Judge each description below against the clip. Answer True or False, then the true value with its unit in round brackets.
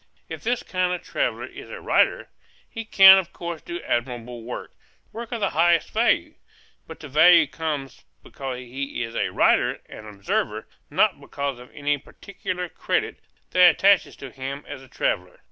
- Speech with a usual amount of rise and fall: False (6.0 semitones)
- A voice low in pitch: False (150 Hz)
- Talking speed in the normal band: True (170 wpm)